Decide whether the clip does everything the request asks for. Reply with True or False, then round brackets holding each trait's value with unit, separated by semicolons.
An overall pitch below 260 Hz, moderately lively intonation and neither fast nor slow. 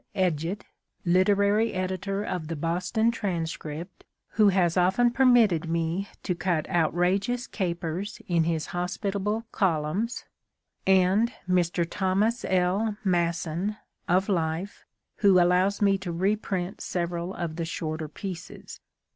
False (185 Hz; 3.0 semitones; 115 wpm)